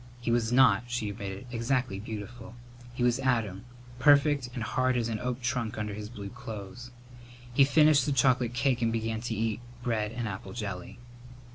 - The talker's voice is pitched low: Yes, low, 120 Hz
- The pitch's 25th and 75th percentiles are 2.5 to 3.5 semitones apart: Yes, average, 2.8 semitones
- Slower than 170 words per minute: No, average, 175 wpm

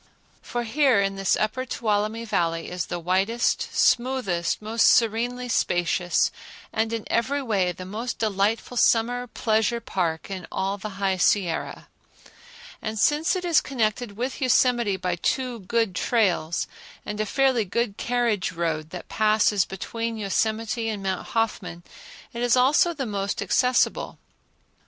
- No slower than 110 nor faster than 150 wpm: Yes, average, 140 wpm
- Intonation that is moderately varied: Yes, average, 3.9 semitones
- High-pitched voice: Yes, high, 220 Hz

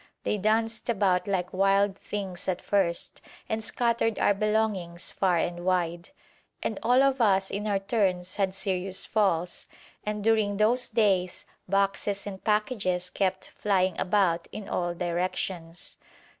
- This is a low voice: No, high, 195 Hz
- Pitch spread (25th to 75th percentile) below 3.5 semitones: Yes, average, 2.7 semitones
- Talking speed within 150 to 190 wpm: No, average, 140 wpm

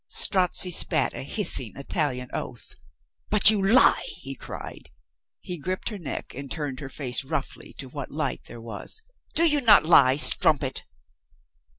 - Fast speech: No, average, 155 wpm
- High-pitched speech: No, medium, 155 Hz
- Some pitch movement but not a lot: No, wide, 6.8 semitones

